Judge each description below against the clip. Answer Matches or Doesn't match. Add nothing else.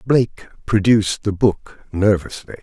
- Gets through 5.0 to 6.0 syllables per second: Doesn't match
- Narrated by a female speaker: Doesn't match